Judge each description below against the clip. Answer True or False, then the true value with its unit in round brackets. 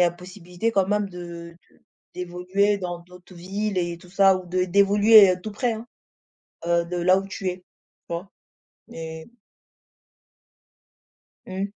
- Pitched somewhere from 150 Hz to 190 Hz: True (185 Hz)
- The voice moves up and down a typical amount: False (2.3 semitones)